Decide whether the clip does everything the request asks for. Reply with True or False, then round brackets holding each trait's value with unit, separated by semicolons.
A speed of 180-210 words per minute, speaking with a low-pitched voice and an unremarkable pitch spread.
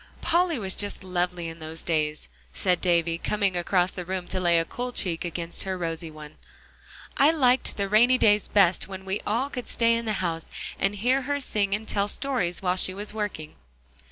False (200 wpm; 190 Hz; 4.1 semitones)